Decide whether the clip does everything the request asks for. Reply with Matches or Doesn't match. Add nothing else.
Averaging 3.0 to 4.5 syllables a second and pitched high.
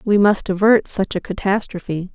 Doesn't match